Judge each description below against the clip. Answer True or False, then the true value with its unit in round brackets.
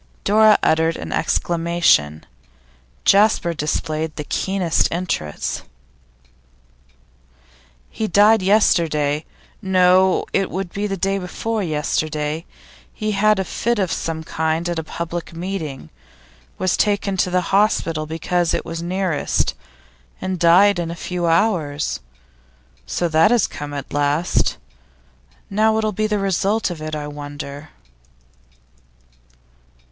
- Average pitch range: True (3.8 semitones)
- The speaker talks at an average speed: False (120 wpm)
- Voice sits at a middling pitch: True (175 Hz)